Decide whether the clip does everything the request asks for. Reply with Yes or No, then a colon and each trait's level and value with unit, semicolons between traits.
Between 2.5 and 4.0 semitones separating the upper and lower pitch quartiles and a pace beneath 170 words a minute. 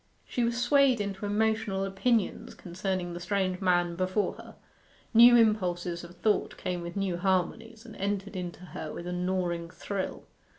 Yes: average, 3.4 semitones; average, 160 wpm